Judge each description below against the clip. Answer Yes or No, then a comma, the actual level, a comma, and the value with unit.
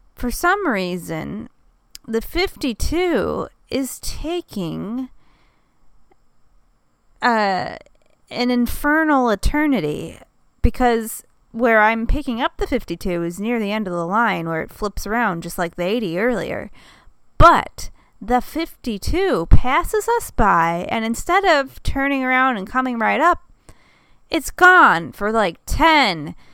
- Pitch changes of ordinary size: No, wide, 6.3 semitones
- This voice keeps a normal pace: No, slow, 120 wpm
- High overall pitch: Yes, high, 245 Hz